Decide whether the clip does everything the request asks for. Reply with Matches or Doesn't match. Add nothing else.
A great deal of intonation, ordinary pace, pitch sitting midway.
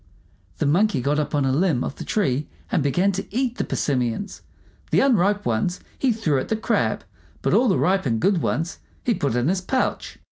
Doesn't match